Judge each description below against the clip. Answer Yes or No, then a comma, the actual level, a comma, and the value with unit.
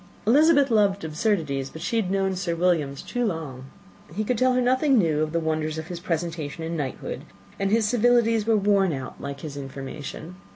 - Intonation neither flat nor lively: No, wide, 6.1 semitones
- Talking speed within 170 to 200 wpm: Yes, average, 195 wpm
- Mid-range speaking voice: Yes, medium, 180 Hz